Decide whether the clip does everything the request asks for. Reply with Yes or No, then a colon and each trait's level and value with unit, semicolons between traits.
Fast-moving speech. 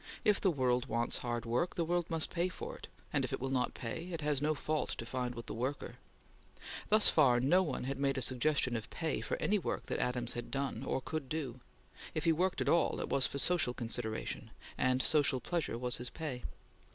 Yes: fast, 225 wpm